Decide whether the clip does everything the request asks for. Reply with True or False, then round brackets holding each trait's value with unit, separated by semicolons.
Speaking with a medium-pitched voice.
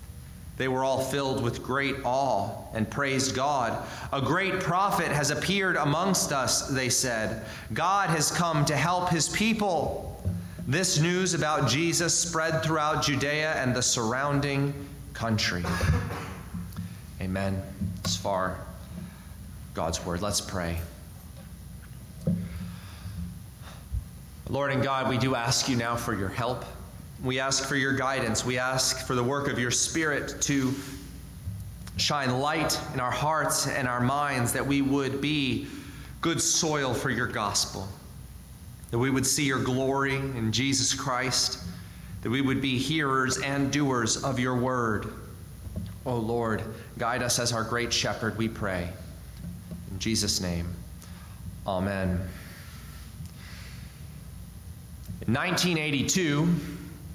False (125 Hz)